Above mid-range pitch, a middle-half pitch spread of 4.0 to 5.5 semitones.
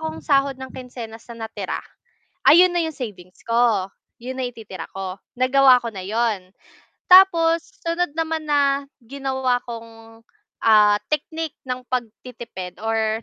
Yes: very high, 250 Hz; average, 4.3 semitones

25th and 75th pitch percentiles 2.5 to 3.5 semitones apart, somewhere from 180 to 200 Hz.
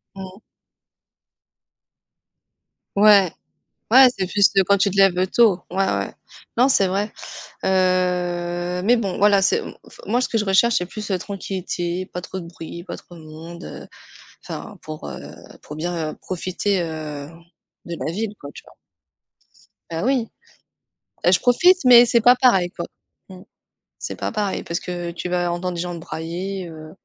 Yes: average, 2.9 semitones; medium, 185 Hz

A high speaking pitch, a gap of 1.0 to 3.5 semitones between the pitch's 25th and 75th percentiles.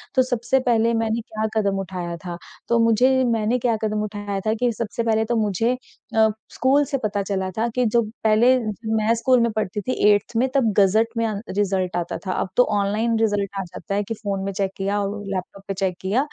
Yes: high, 215 Hz; average, 2.7 semitones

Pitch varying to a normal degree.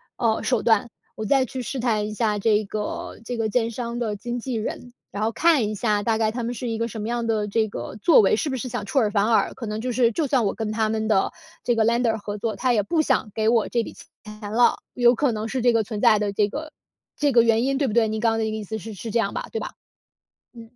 No: narrow, 2.1 semitones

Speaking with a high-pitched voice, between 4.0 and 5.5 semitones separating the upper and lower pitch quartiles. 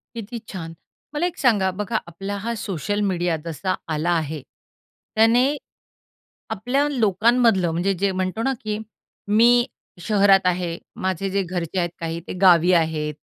Yes: high, 195 Hz; average, 4.5 semitones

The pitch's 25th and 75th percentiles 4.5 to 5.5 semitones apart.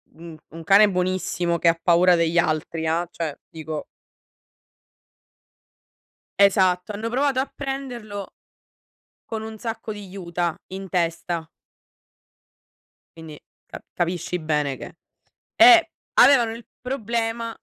Yes: average, 5.2 semitones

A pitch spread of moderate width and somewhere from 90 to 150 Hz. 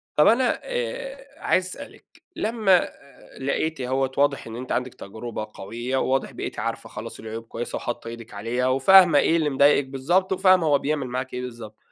No: wide, 7.1 semitones; low, 135 Hz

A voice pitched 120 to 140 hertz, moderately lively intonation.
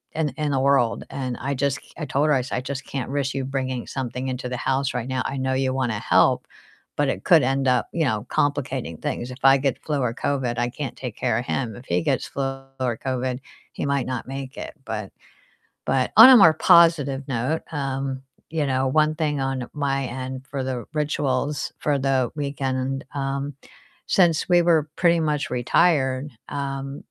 No: low, 135 Hz; narrow, 1.9 semitones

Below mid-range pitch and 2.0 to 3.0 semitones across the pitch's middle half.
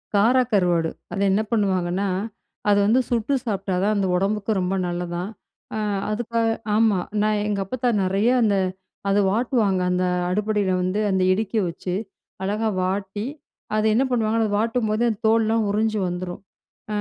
No: high, 205 Hz; average, 2.7 semitones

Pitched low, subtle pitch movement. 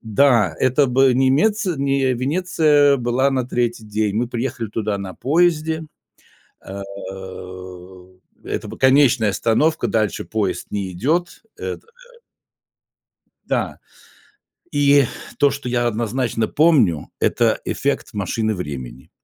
No: low, 125 Hz; average, 4.8 semitones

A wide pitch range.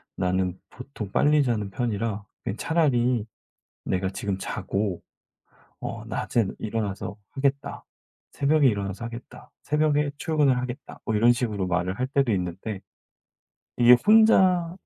Yes: wide, 5.9 semitones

